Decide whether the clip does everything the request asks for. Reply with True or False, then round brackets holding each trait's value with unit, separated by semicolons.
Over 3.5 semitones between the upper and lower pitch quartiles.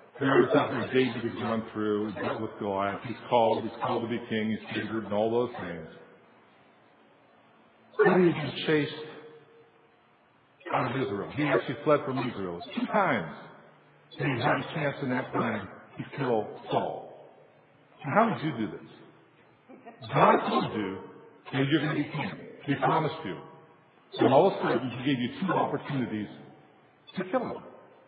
True (5.3 semitones)